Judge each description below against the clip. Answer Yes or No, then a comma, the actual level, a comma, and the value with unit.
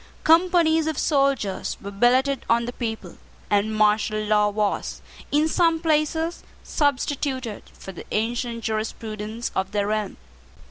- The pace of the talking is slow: Yes, slow, 130 wpm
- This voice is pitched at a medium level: No, high, 235 Hz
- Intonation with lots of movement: Yes, wide, 5.7 semitones